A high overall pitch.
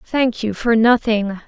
Yes: high, 225 Hz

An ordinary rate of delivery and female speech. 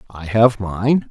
No: average, 165 wpm; male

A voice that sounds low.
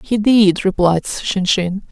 No: high, 195 Hz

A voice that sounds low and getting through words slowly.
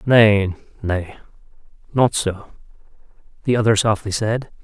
Yes: low, 105 Hz; slow, 105 wpm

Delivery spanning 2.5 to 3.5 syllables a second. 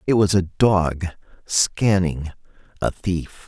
Yes: 3.4 syllables/s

